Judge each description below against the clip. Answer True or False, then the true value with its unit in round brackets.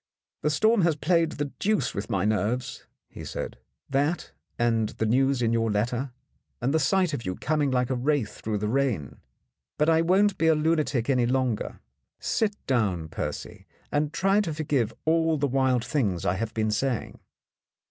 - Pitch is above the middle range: False (135 Hz)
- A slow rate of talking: False (180 wpm)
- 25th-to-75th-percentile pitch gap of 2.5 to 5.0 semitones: False (5.5 semitones)